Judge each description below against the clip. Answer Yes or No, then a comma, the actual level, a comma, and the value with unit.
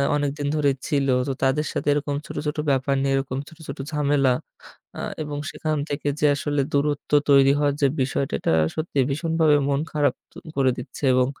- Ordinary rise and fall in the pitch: No, narrow, 1.4 semitones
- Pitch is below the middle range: No, medium, 145 Hz